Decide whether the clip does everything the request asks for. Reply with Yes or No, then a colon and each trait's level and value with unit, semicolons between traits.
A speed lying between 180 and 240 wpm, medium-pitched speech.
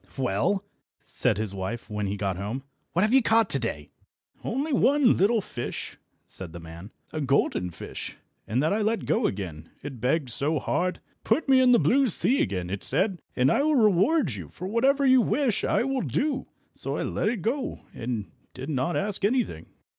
Yes: average, 195 wpm; medium, 165 Hz